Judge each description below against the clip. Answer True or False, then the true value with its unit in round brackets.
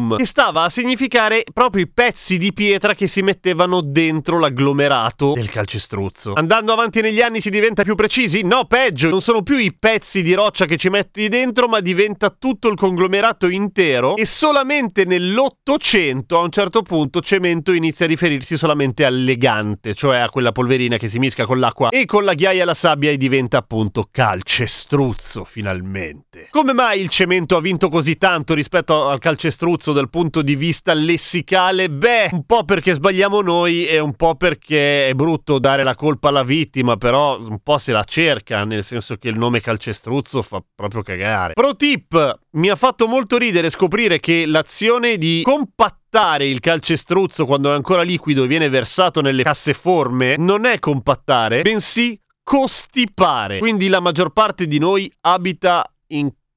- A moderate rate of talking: False (175 wpm)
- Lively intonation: True (6.4 semitones)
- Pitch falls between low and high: True (170 Hz)